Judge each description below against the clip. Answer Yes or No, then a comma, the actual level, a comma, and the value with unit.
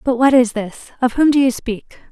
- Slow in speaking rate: No, fast, 225 wpm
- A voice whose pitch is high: Yes, very high, 250 Hz